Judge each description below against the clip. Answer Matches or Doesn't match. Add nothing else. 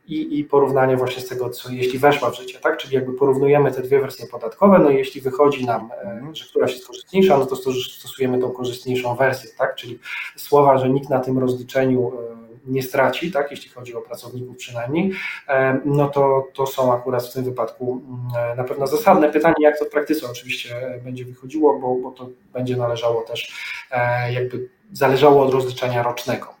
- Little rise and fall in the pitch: Matches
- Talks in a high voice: Doesn't match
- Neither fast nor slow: Doesn't match